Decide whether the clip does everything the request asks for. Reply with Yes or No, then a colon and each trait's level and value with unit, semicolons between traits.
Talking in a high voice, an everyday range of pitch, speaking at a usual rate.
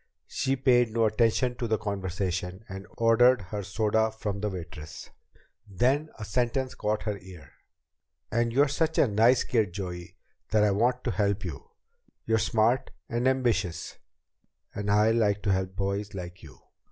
No: low, 105 Hz; average, 3.5 semitones; average, 165 wpm